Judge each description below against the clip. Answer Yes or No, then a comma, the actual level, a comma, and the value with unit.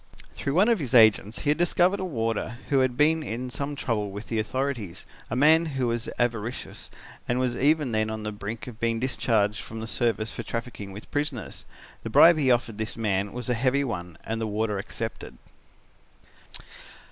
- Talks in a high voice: No, low, 120 Hz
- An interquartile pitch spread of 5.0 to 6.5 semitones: No, average, 4.0 semitones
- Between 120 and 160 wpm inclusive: No, average, 190 wpm